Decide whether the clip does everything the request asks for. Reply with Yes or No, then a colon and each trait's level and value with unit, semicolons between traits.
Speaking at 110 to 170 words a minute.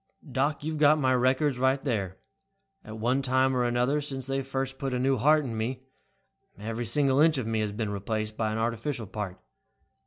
No: average, 190 wpm